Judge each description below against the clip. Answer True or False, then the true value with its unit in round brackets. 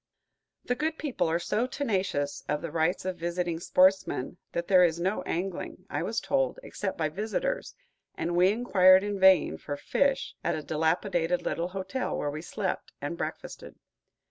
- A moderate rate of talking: True (170 wpm)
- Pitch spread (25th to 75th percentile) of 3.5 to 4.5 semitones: True (3.8 semitones)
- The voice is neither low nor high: True (180 Hz)